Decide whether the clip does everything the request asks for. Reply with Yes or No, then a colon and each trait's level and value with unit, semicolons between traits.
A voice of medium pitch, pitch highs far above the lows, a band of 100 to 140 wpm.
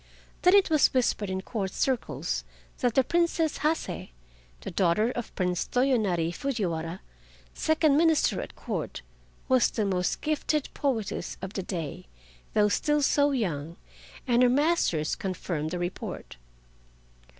No: high, 230 Hz; wide, 8.1 semitones; slow, 135 wpm